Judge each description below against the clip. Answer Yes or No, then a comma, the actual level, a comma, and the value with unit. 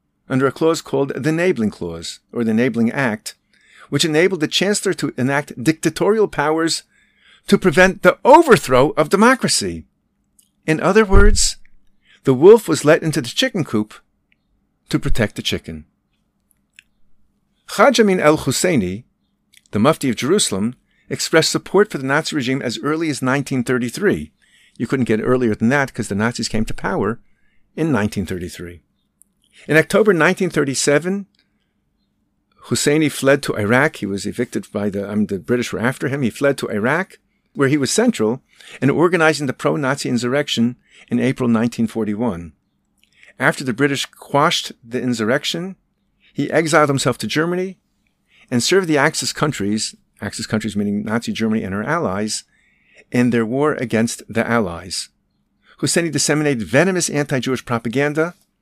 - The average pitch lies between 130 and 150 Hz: Yes, low, 135 Hz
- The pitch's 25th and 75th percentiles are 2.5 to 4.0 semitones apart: No, wide, 5.6 semitones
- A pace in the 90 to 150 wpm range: Yes, average, 145 wpm